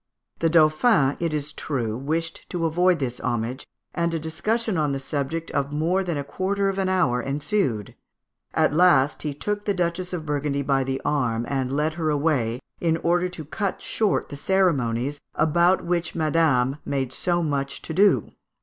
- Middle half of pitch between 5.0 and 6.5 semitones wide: No, average, 4.2 semitones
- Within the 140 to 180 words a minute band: Yes, average, 175 wpm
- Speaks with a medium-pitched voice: Yes, medium, 155 Hz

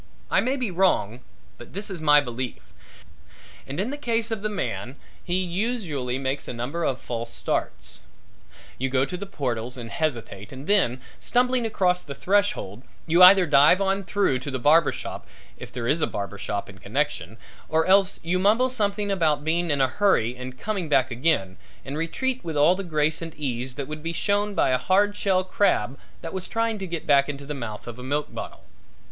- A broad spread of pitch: Yes, wide, 7.3 semitones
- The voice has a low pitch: No, medium, 155 Hz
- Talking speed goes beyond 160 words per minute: Yes, average, 200 wpm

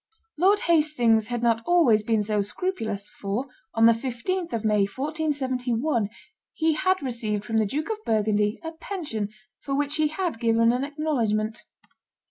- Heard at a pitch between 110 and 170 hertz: No, high, 240 Hz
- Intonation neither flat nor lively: No, wide, 6.1 semitones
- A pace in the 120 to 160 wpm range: Yes, average, 155 wpm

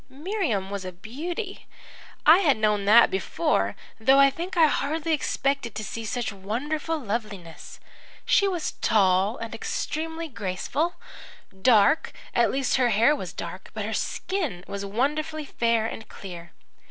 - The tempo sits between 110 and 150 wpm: Yes, average, 145 wpm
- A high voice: Yes, high, 235 Hz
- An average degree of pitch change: No, wide, 7.5 semitones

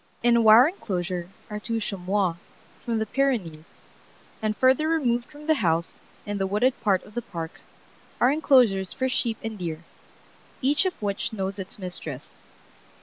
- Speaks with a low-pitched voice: No, high, 215 Hz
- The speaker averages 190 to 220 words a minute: No, average, 160 wpm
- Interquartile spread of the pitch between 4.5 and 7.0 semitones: Yes, average, 5.1 semitones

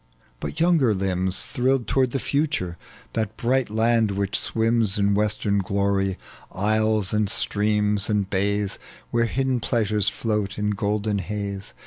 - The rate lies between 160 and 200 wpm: No, slow, 135 wpm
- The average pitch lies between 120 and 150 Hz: No, low, 105 Hz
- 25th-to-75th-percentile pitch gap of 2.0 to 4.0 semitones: Yes, narrow, 2.5 semitones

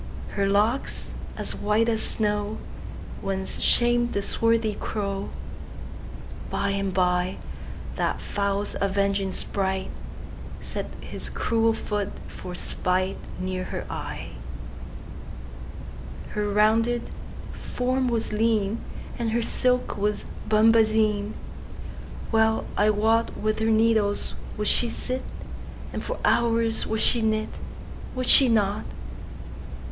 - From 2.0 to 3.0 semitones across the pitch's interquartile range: Yes, narrow, 2.4 semitones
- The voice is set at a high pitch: Yes, high, 215 Hz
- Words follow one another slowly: Yes, slow, 90 wpm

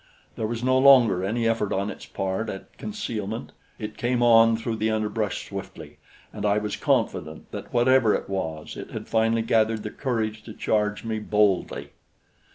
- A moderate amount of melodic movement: No, narrow, 1.7 semitones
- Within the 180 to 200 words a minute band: No, average, 170 wpm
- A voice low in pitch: Yes, low, 110 Hz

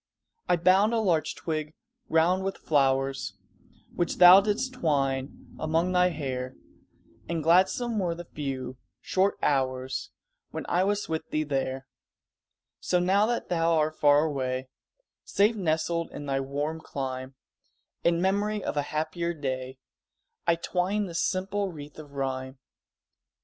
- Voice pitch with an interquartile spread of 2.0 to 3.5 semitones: No, average, 5.1 semitones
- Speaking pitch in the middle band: Yes, medium, 160 Hz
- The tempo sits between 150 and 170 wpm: No, average, 140 wpm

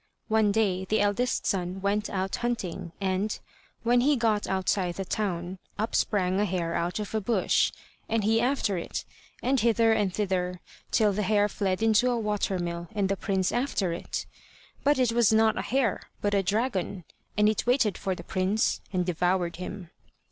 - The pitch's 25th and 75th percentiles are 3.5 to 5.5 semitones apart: No, average, 3.1 semitones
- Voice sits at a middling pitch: No, high, 205 Hz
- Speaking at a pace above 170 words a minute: Yes, average, 185 wpm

